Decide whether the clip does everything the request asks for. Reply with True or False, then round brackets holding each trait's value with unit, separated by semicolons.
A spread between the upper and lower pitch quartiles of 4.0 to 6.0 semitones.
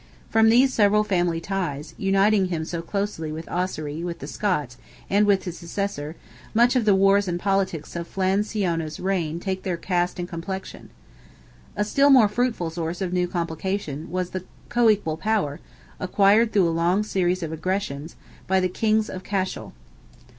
False (3.3 semitones)